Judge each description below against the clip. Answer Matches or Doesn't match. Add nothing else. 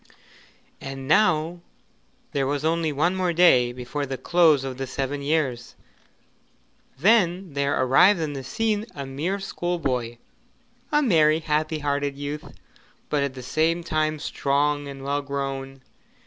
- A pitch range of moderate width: Matches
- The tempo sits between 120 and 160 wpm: Matches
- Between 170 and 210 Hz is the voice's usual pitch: Doesn't match